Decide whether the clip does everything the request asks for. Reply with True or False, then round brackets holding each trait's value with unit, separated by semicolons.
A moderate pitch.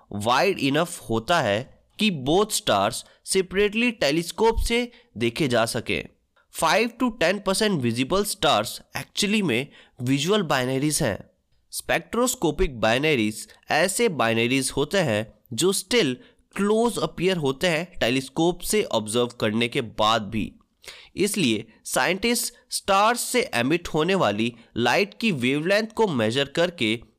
True (170 Hz)